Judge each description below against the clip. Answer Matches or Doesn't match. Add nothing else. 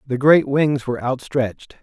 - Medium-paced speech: Matches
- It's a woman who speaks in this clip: Doesn't match